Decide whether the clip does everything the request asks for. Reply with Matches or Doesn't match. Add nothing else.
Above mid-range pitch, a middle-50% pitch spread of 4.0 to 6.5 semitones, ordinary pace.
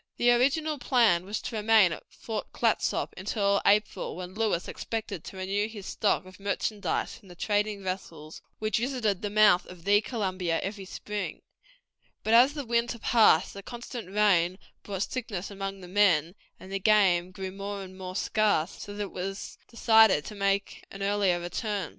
Doesn't match